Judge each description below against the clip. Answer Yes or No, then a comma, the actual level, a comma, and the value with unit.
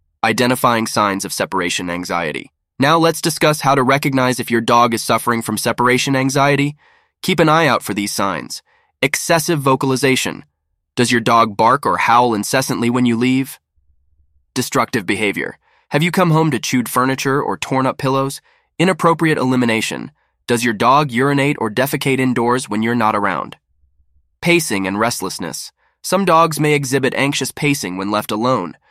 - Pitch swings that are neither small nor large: Yes, average, 4.1 semitones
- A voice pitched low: Yes, low, 125 Hz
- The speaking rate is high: No, average, 160 wpm